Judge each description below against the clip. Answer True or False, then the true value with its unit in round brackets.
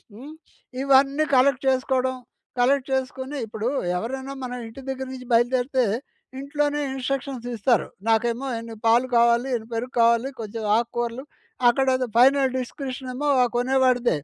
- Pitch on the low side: False (255 Hz)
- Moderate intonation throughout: False (2.2 semitones)